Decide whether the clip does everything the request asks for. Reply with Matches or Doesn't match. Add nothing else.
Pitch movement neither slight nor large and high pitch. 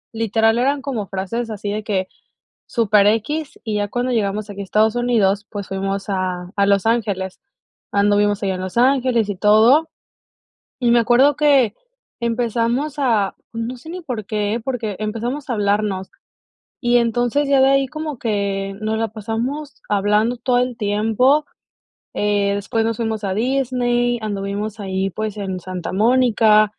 Matches